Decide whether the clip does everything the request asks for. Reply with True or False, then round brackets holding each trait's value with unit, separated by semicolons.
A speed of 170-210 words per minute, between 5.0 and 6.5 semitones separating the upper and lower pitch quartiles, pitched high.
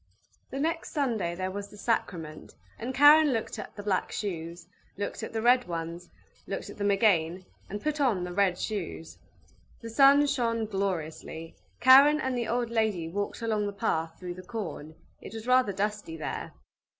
True (175 wpm; 5.4 semitones; 205 Hz)